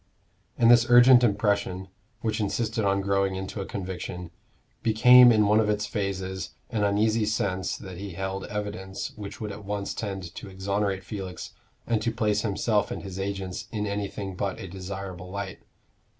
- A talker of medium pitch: No, low, 100 Hz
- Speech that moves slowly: No, average, 165 wpm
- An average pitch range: No, narrow, 2.0 semitones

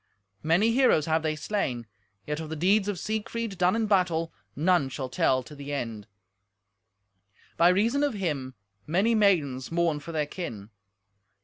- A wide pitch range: Yes, wide, 5.8 semitones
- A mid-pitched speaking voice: Yes, medium, 165 Hz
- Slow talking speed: No, average, 155 wpm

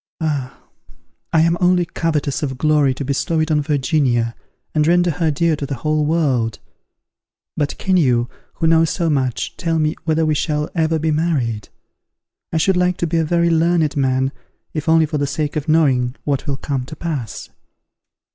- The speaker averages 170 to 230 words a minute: Yes, average, 185 wpm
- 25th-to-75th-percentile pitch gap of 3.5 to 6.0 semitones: No, average, 2.9 semitones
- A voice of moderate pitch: Yes, medium, 155 Hz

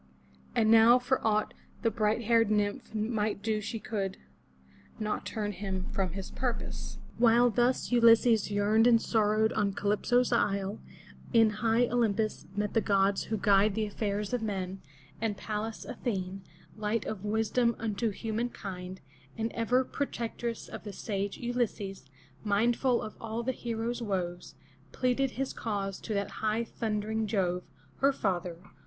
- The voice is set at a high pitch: Yes, high, 215 Hz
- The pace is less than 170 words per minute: Yes, average, 150 wpm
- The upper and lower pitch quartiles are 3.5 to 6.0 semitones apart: No, narrow, 2.5 semitones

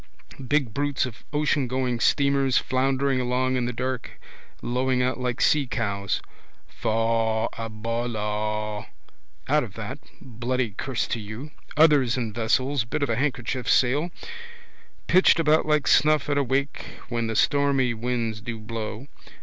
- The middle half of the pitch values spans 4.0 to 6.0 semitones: No, average, 3.4 semitones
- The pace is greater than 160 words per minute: No, average, 140 wpm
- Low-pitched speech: Yes, low, 125 Hz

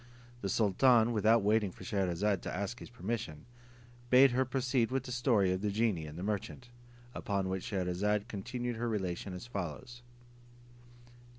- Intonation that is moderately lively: Yes, average, 4.1 semitones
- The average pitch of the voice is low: Yes, low, 105 Hz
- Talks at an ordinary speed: Yes, average, 160 wpm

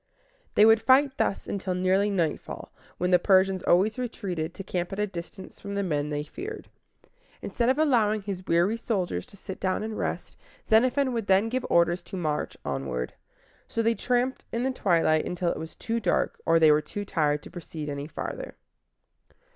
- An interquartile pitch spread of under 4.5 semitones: No, average, 4.9 semitones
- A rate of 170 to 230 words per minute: Yes, average, 185 wpm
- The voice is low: No, high, 190 Hz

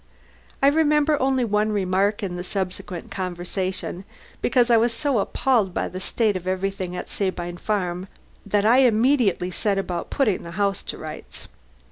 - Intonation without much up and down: No, average, 4.3 semitones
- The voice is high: Yes, high, 200 Hz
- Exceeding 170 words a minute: No, average, 160 wpm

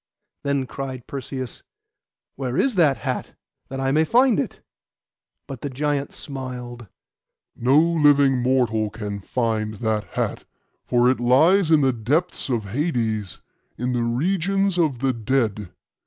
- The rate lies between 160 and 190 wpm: No, average, 140 wpm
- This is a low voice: Yes, low, 130 Hz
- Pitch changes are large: No, average, 3.9 semitones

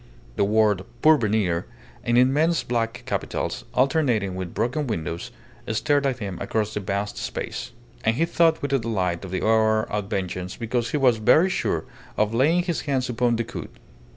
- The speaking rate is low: No, average, 165 wpm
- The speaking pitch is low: Yes, low, 115 Hz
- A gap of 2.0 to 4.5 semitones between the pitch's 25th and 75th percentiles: No, average, 4.9 semitones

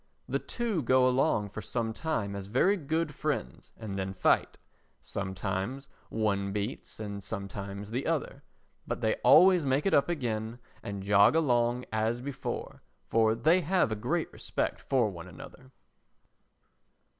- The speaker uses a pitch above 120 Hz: No, low, 115 Hz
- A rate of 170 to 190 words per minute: No, average, 145 wpm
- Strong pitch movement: Yes, wide, 5.9 semitones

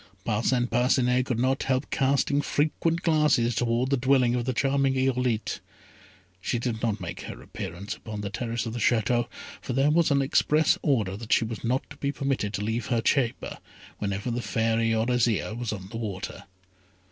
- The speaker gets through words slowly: No, average, 185 wpm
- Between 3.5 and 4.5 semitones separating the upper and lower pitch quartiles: No, average, 3.1 semitones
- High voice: No, low, 120 Hz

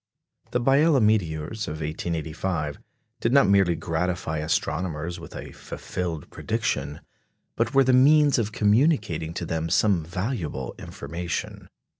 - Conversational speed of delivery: No, slow, 125 wpm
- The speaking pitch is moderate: No, very low, 90 Hz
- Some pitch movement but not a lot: No, wide, 6.2 semitones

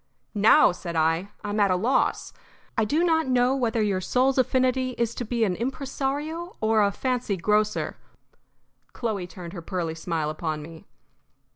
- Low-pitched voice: No, high, 220 Hz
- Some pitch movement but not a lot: No, wide, 6.1 semitones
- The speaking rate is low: No, average, 165 wpm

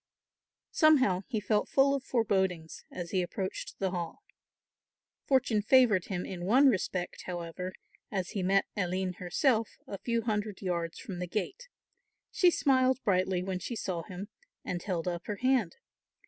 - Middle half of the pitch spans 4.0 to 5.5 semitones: Yes, average, 4.5 semitones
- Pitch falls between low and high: No, high, 195 Hz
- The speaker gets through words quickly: No, average, 155 wpm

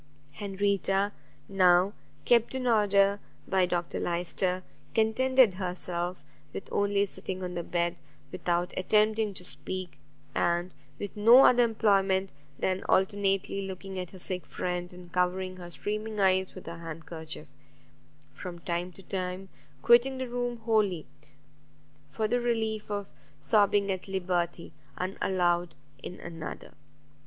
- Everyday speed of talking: No, slow, 130 wpm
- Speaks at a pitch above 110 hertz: Yes, high, 190 Hz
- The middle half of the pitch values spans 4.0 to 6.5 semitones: No, narrow, 2.6 semitones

